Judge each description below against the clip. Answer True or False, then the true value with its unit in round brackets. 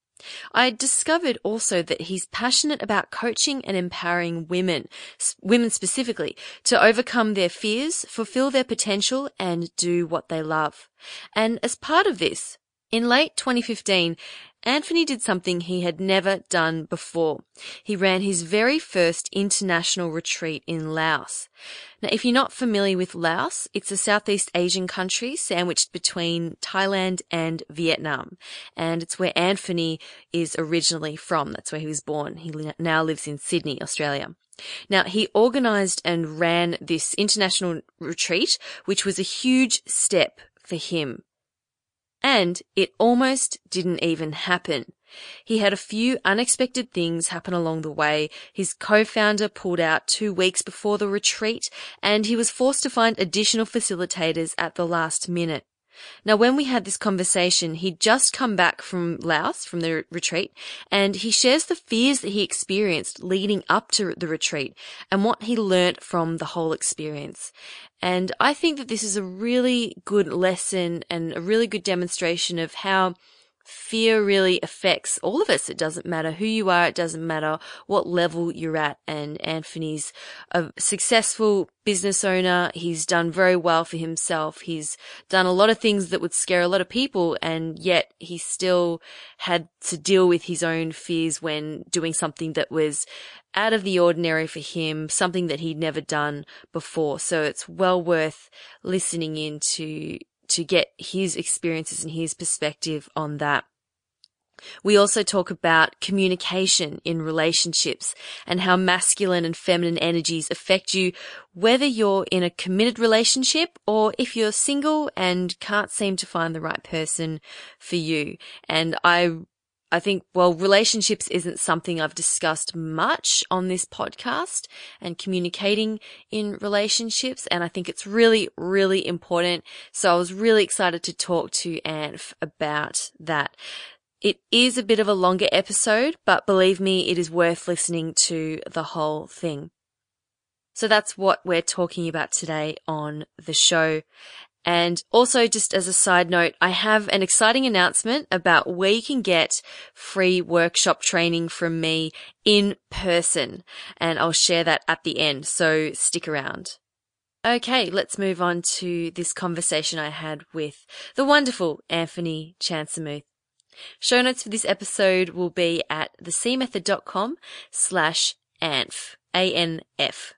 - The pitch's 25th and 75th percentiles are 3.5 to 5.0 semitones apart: True (4.0 semitones)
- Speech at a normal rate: True (155 wpm)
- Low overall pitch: False (180 Hz)